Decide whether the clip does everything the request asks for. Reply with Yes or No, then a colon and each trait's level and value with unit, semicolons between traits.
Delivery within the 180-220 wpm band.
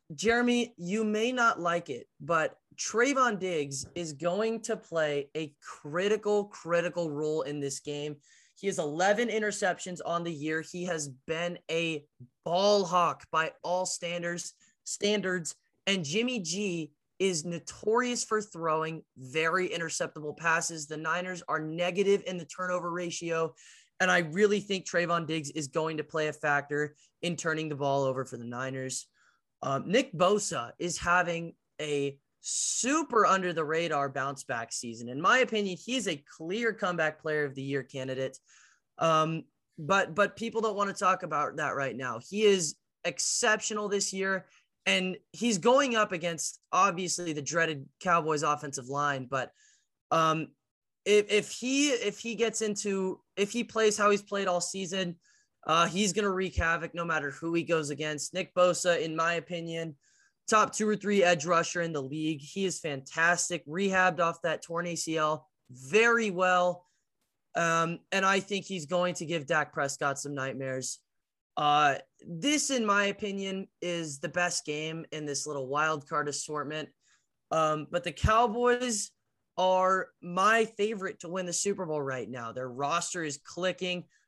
No: average, 160 wpm